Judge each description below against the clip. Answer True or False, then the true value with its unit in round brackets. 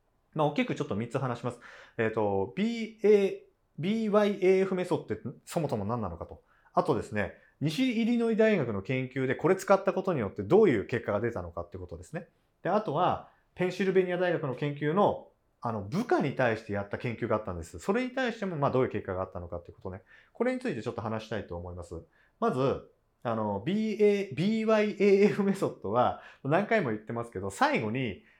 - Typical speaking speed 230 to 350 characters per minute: False (405 characters per minute)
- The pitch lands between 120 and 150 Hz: True (135 Hz)